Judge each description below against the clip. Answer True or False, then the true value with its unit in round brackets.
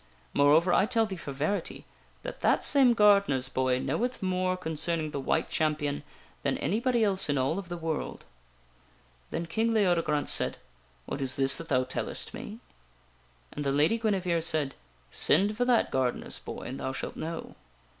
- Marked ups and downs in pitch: True (6.0 semitones)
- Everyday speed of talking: True (170 wpm)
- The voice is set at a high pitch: False (165 Hz)